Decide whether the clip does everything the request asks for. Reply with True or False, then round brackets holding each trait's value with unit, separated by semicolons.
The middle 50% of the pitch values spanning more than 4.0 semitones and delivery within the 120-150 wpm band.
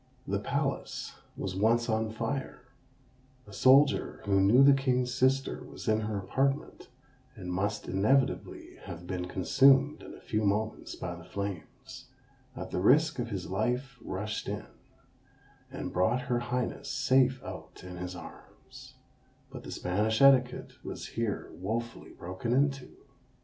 True (5.1 semitones; 145 wpm)